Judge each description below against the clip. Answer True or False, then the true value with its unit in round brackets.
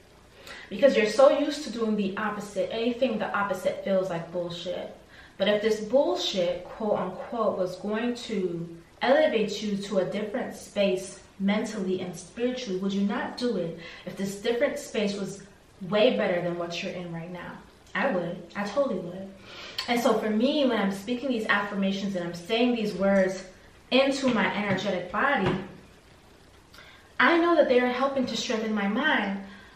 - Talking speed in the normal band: True (165 wpm)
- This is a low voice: False (205 Hz)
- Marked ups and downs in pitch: False (4.3 semitones)